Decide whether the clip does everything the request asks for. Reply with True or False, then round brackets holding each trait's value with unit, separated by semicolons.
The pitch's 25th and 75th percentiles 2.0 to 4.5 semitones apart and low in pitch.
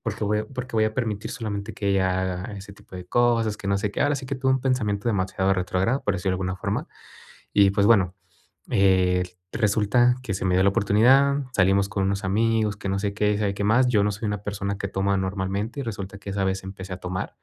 True (2.5 semitones; 100 Hz)